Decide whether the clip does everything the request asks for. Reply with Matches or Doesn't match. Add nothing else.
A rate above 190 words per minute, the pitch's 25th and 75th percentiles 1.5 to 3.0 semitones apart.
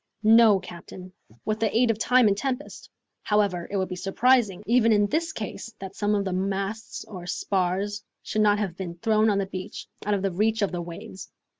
Matches